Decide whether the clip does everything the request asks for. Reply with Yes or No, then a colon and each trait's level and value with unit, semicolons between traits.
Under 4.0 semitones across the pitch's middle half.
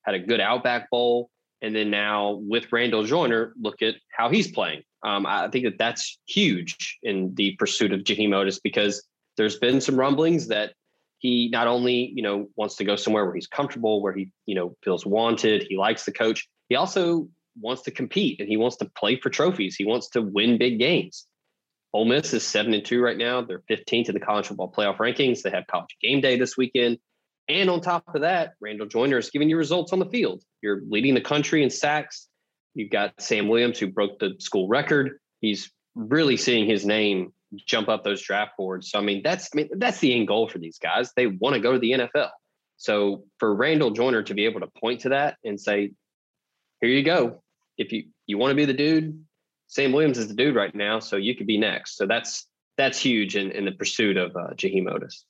No: average, 4.8 semitones